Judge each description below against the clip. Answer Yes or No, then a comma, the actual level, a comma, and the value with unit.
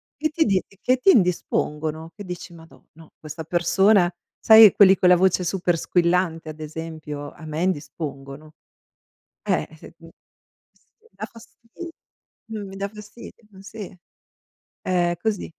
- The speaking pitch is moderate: Yes, medium, 180 Hz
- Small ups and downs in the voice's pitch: No, average, 4.1 semitones